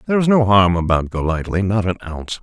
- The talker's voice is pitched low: Yes, low, 100 Hz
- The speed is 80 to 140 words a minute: No, average, 200 wpm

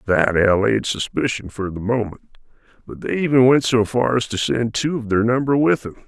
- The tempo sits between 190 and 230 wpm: Yes, fast, 205 wpm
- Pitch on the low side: Yes, low, 115 Hz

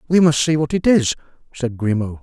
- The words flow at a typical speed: No, fast, 215 wpm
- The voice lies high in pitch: No, medium, 140 Hz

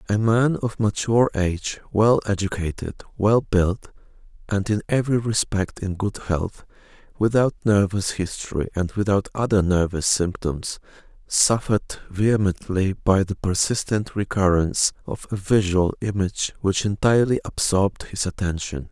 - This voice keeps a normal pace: No, slow, 125 wpm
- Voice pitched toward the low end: Yes, low, 100 Hz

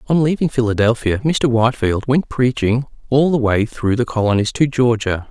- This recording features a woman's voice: No, male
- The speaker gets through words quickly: No, average, 170 wpm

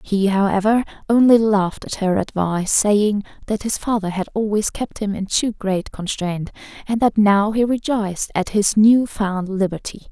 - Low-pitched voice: No, high, 205 Hz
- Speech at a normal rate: Yes, average, 170 wpm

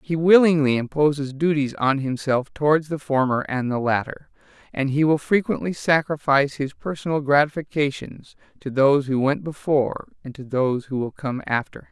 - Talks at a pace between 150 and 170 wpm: Yes, average, 165 wpm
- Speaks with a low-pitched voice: No, medium, 145 Hz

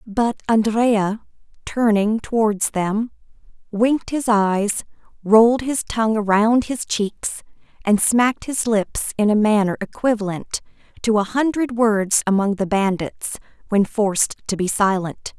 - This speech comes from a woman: Yes, female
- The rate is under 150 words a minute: Yes, slow, 135 wpm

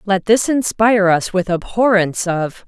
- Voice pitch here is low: No, high, 200 Hz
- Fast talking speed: No, average, 155 wpm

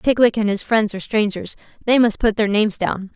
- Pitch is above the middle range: Yes, high, 215 Hz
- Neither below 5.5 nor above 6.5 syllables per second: Yes, 5.9 syllables/s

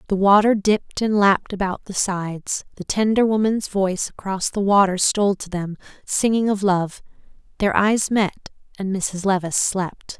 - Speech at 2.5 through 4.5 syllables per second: No, 4.8 syllables/s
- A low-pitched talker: No, high, 195 Hz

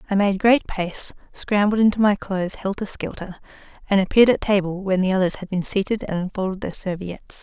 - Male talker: No, female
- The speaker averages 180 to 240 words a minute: Yes, average, 195 wpm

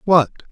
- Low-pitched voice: No, medium, 165 Hz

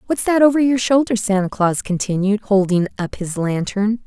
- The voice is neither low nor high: No, high, 210 Hz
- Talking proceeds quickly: No, average, 175 wpm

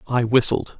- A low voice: Yes, low, 120 Hz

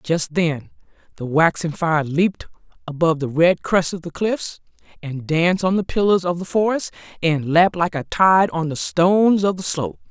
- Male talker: No, female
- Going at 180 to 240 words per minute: Yes, average, 190 wpm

